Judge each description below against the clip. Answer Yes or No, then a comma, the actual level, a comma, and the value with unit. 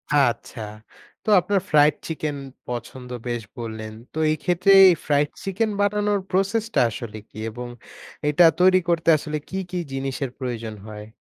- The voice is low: No, medium, 150 Hz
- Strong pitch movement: Yes, wide, 7.2 semitones